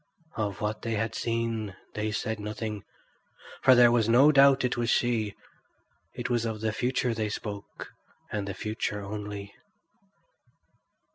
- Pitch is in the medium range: No, low, 110 Hz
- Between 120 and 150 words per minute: Yes, average, 145 wpm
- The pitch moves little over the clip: Yes, narrow, 2.3 semitones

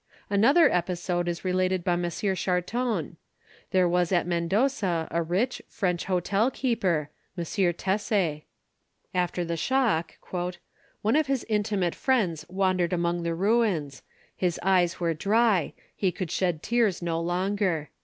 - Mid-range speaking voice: Yes, medium, 180 Hz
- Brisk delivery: No, slow, 135 wpm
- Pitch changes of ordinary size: Yes, average, 3.2 semitones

